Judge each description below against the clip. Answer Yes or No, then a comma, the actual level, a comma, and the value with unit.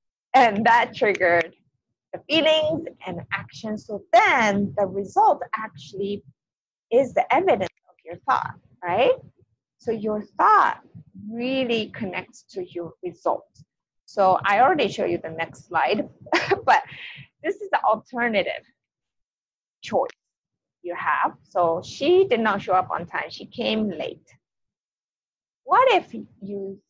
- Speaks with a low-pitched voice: No, high, 215 Hz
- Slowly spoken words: Yes, slow, 125 wpm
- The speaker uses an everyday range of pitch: No, wide, 8.2 semitones